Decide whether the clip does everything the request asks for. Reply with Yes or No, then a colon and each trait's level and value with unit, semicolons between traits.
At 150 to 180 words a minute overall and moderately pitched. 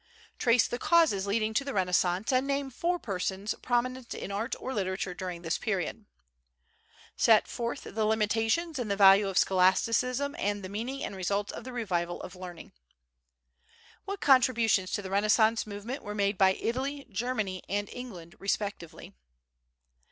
No: average, 155 wpm; high, 215 Hz